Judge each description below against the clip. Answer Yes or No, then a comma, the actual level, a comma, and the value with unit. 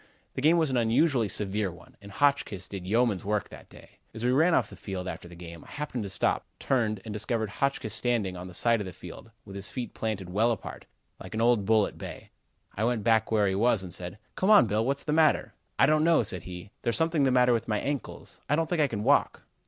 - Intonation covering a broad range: No, average, 4.8 semitones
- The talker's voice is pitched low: Yes, low, 110 Hz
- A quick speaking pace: Yes, fast, 250 wpm